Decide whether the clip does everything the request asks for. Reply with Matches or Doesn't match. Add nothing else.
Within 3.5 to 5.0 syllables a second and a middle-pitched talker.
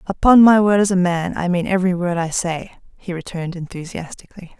Doesn't match